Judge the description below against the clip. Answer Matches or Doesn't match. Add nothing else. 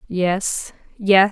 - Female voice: Matches